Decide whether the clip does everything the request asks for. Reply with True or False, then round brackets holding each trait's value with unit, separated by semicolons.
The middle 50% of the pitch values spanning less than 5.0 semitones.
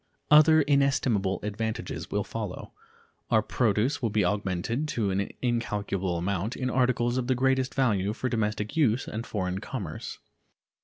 True (4.2 semitones)